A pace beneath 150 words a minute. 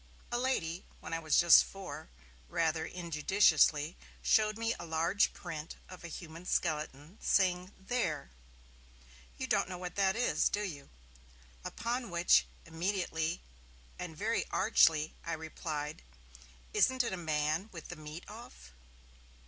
Yes: slow, 135 wpm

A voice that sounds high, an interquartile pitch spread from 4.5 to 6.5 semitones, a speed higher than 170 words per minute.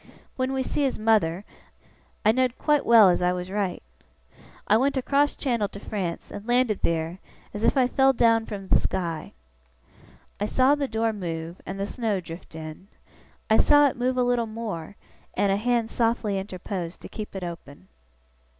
Yes: high, 215 Hz; average, 5.1 semitones; average, 180 wpm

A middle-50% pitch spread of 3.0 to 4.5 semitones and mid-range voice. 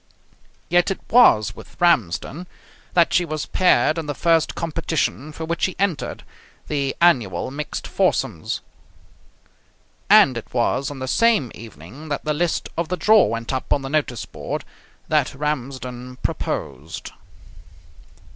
No: average, 5.0 semitones; medium, 150 Hz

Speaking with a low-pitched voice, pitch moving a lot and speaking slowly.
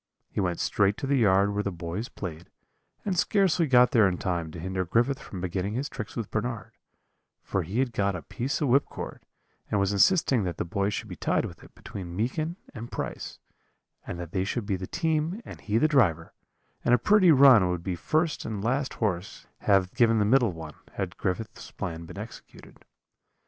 No: low, 105 Hz; wide, 5.9 semitones; average, 200 wpm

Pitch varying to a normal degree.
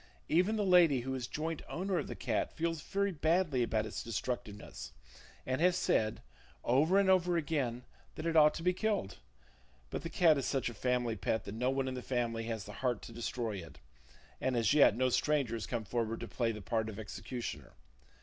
No: wide, 6.2 semitones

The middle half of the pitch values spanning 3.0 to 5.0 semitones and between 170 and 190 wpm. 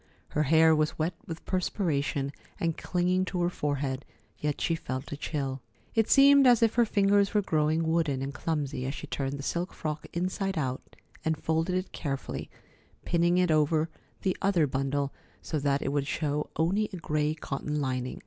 Yes: average, 4.1 semitones; average, 180 wpm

